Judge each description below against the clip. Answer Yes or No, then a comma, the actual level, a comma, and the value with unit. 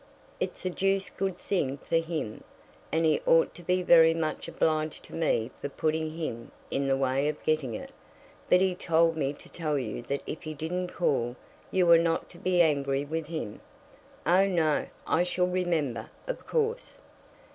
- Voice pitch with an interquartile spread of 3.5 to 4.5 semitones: Yes, average, 3.8 semitones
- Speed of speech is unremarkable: Yes, average, 180 wpm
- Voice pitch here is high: No, medium, 160 Hz